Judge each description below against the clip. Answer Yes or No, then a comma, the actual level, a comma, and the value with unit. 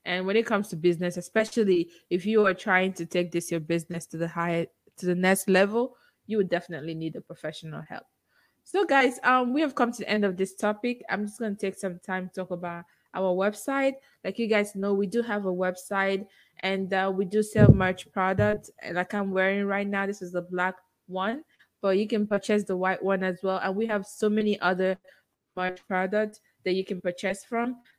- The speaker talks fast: Yes, fast, 220 wpm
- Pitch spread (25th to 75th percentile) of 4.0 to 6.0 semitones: No, narrow, 2.6 semitones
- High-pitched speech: Yes, high, 195 Hz